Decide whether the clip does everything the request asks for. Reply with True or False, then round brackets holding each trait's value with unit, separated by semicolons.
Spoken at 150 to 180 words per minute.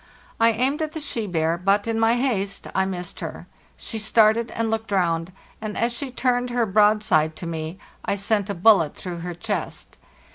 False (190 wpm)